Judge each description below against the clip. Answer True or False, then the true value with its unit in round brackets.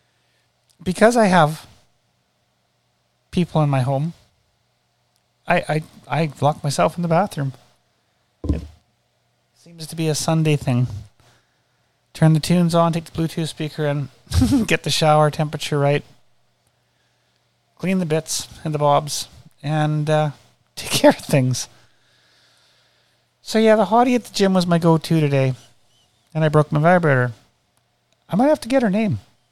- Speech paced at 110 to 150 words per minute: True (145 wpm)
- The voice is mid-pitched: True (150 Hz)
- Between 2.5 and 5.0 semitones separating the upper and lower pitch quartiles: False (5.4 semitones)